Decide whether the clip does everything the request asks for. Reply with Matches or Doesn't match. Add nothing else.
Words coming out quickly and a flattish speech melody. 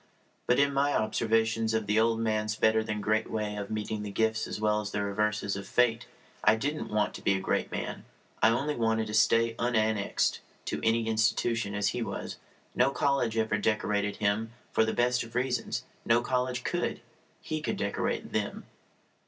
Doesn't match